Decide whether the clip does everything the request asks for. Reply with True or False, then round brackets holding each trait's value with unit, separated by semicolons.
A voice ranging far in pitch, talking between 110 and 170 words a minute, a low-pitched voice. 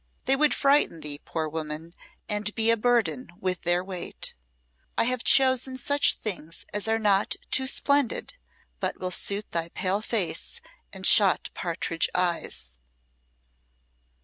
False (6.2 semitones; 140 wpm; 200 Hz)